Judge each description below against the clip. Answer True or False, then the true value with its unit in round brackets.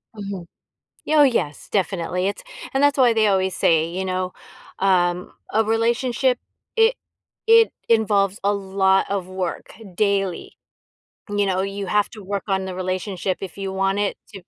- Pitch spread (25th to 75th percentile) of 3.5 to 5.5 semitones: False (2.5 semitones)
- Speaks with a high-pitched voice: True (195 Hz)